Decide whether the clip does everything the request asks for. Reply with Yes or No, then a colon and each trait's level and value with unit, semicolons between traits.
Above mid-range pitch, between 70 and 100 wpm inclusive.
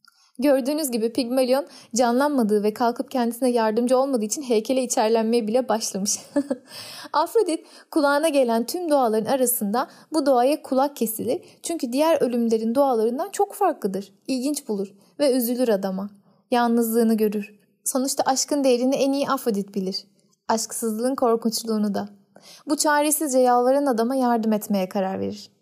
No: high, 245 Hz; average, 130 wpm